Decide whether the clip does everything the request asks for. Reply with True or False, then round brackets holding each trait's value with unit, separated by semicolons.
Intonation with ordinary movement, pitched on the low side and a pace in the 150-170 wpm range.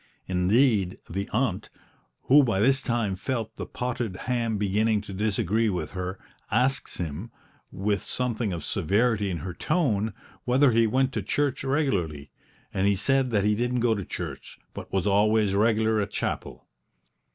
True (4.1 semitones; 110 Hz; 160 wpm)